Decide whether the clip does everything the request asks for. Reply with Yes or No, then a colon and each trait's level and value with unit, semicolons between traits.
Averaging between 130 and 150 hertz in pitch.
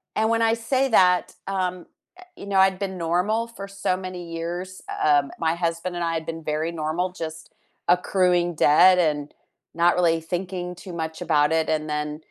No: medium, 175 Hz